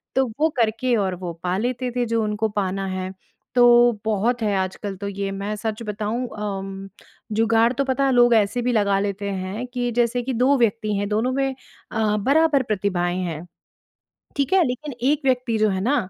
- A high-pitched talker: Yes, high, 220 Hz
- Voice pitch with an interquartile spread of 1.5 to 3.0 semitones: No, average, 3.7 semitones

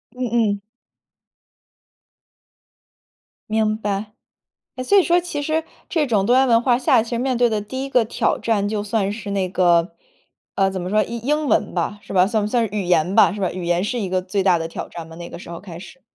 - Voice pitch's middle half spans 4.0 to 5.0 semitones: Yes, average, 4.5 semitones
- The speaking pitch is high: Yes, high, 210 Hz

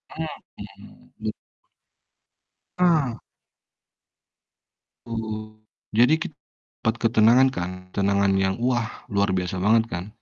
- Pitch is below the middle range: Yes, low, 110 Hz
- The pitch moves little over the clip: No, average, 3.3 semitones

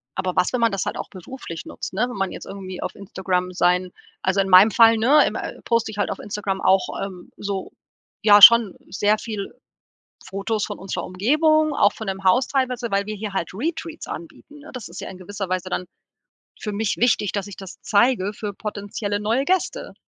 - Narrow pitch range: No, average, 3.4 semitones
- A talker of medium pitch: No, high, 205 Hz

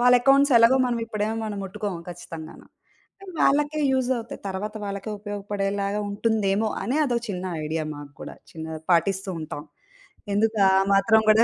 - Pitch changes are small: No, average, 3.1 semitones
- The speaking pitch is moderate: No, high, 205 Hz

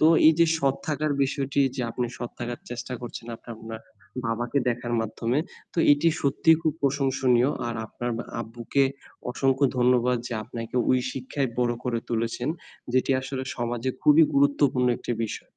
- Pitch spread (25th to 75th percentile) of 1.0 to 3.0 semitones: Yes, narrow, 2.6 semitones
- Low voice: Yes, low, 125 Hz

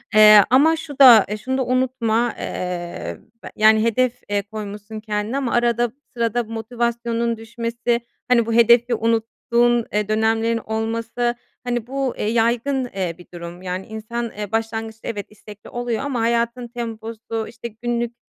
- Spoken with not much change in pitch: Yes, narrow, 1.7 semitones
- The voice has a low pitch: No, high, 230 Hz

